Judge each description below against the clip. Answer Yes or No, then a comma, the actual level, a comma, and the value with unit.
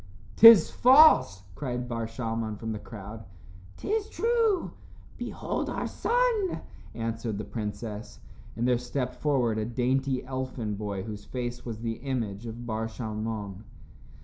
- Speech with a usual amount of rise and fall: Yes, average, 3.3 semitones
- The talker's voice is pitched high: No, low, 115 Hz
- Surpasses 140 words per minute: No, slow, 135 wpm